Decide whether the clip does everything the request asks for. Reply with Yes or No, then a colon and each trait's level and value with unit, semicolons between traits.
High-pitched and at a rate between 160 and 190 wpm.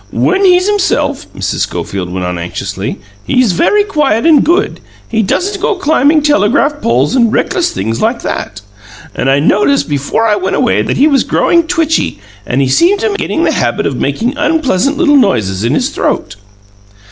Yes: very high, 260 Hz; average, 180 wpm